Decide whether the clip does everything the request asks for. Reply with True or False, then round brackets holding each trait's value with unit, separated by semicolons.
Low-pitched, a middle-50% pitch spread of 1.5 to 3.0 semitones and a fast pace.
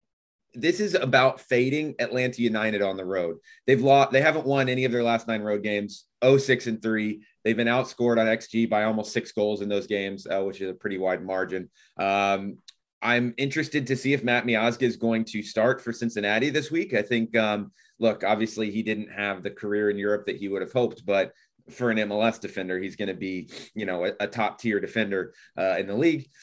False (110 Hz; 3.7 semitones; 220 wpm)